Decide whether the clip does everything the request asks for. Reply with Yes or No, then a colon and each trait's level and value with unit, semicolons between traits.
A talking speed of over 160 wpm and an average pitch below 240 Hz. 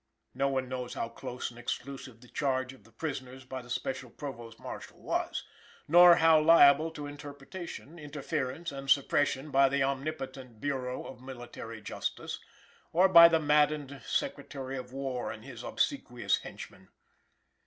No: average, 150 wpm; low, 135 Hz